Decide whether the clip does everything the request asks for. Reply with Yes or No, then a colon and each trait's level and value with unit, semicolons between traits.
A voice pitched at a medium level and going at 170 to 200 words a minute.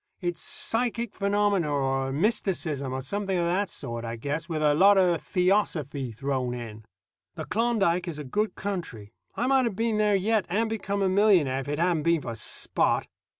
Yes: medium, 175 Hz; average, 185 wpm